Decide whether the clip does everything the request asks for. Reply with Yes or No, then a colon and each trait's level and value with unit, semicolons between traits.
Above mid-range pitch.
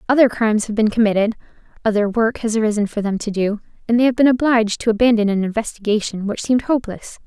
Yes: high, 220 Hz